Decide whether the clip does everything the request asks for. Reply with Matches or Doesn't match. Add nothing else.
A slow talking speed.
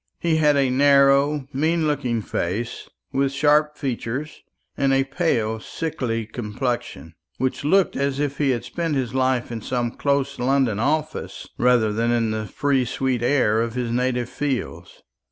Doesn't match